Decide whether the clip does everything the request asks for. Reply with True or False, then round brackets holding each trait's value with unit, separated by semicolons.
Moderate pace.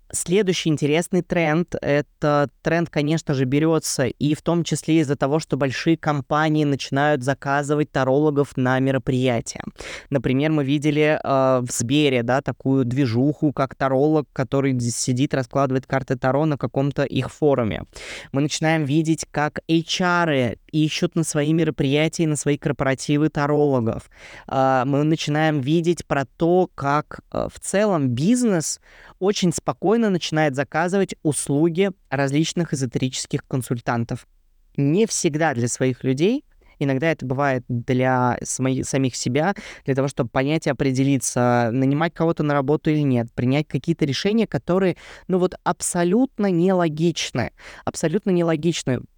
True (130 wpm)